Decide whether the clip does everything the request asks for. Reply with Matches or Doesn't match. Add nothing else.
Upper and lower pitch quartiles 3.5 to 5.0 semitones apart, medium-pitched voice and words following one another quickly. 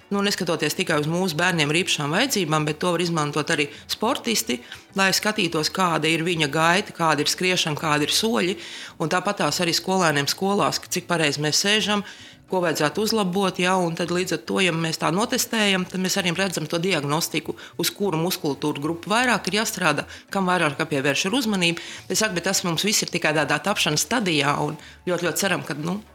Doesn't match